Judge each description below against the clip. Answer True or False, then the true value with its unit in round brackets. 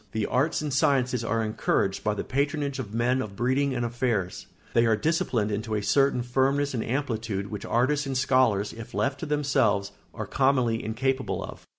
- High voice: False (125 Hz)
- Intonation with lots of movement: False (3.8 semitones)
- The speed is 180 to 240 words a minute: True (185 wpm)